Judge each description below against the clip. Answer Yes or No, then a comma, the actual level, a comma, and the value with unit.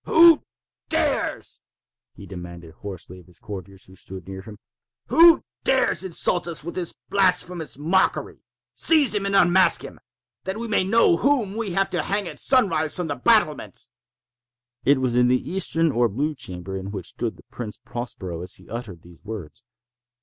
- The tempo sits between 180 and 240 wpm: No, average, 165 wpm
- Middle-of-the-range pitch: Yes, medium, 145 Hz